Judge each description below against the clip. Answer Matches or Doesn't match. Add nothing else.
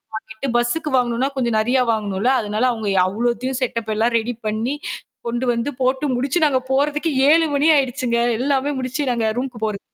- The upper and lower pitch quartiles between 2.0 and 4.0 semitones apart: Matches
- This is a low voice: Doesn't match